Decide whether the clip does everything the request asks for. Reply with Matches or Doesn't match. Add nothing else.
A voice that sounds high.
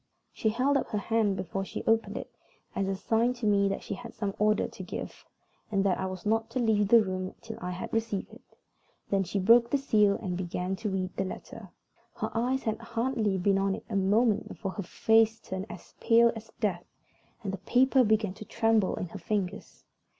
Matches